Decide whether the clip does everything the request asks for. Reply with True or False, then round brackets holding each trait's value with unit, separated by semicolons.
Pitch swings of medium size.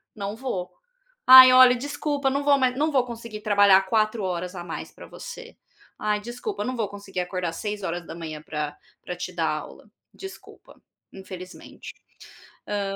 False (5.8 semitones)